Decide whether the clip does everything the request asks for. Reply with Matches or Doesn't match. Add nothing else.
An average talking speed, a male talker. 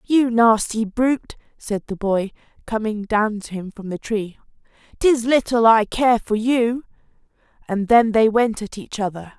Doesn't match